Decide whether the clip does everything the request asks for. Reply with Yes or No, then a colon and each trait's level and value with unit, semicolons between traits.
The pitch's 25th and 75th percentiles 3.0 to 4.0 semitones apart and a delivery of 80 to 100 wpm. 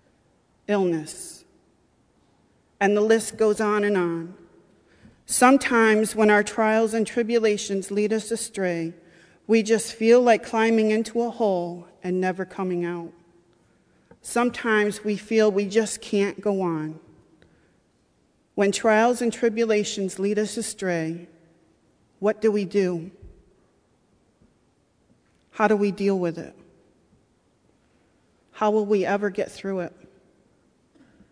No: average, 3.4 semitones; slow, 115 wpm